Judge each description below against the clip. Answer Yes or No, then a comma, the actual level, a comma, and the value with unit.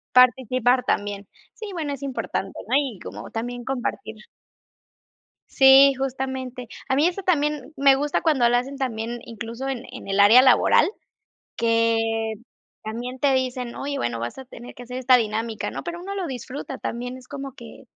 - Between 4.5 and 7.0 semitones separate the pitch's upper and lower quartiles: No, average, 2.9 semitones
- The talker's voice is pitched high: Yes, very high, 250 Hz